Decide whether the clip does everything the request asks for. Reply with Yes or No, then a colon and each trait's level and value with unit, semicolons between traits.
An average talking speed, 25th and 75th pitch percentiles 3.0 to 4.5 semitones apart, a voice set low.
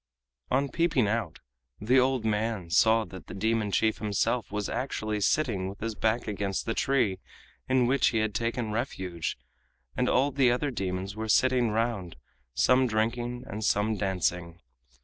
Yes: average, 160 wpm; average, 3.5 semitones; low, 110 Hz